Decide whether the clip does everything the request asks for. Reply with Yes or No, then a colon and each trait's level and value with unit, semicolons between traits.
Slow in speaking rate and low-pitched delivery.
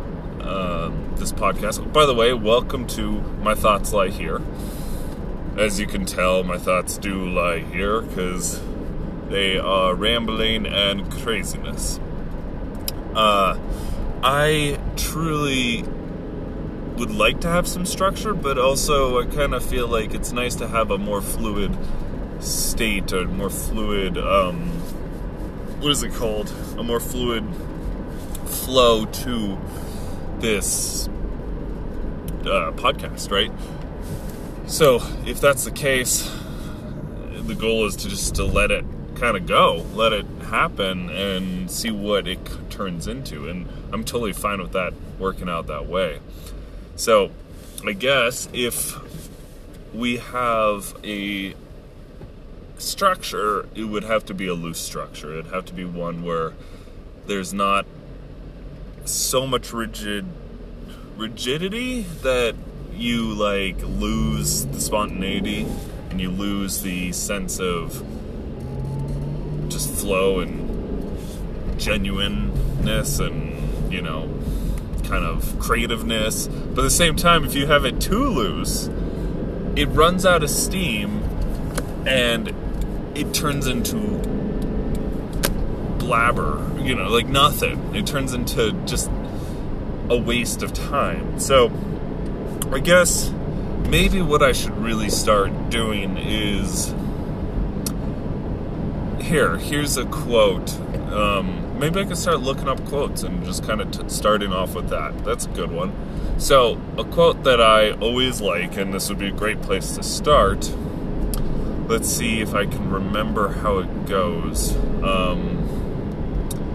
Yes: slow, 125 wpm; low, 100 Hz